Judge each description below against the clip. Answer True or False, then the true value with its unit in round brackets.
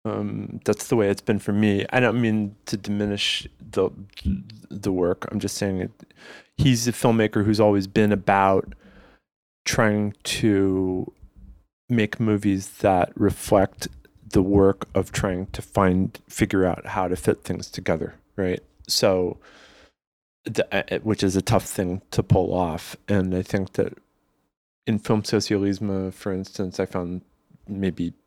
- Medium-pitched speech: False (100 Hz)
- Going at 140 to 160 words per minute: True (145 wpm)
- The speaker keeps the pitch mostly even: True (2.1 semitones)